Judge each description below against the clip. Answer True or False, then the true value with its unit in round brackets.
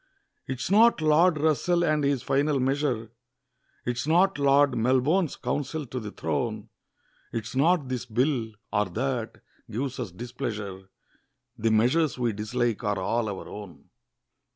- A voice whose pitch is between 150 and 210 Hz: False (125 Hz)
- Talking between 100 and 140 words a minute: True (135 wpm)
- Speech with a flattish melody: False (4.8 semitones)